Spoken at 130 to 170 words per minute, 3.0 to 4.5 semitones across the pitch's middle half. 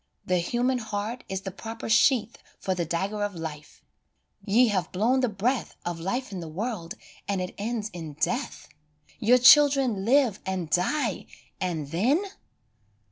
No: average, 155 wpm; average, 5.3 semitones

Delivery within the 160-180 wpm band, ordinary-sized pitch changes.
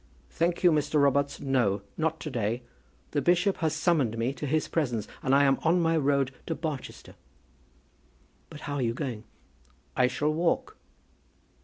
Yes: average, 165 wpm; average, 3.9 semitones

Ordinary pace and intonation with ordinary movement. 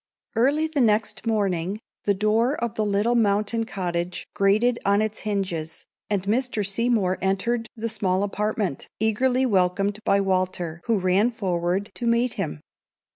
Yes: average, 150 wpm; average, 3.3 semitones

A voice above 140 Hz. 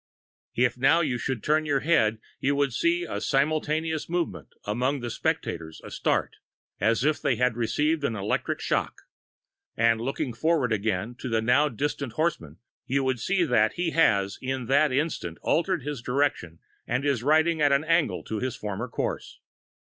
No: low, 135 Hz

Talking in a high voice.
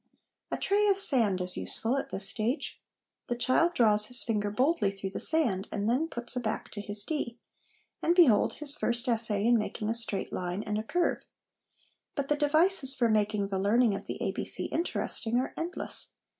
Yes: high, 235 Hz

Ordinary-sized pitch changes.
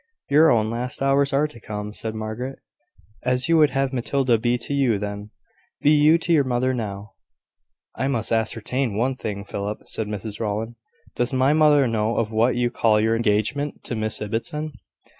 Yes: average, 4.0 semitones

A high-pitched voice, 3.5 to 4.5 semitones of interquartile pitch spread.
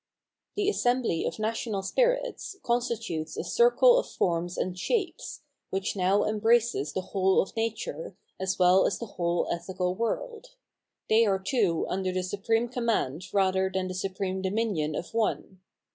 Yes: high, 195 Hz; average, 4.2 semitones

